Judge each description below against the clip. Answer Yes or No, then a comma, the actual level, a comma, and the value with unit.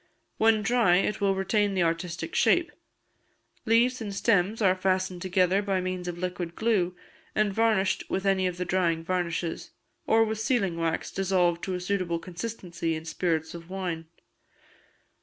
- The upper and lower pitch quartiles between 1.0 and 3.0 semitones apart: Yes, average, 2.7 semitones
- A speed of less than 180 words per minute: Yes, average, 160 wpm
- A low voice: No, medium, 185 Hz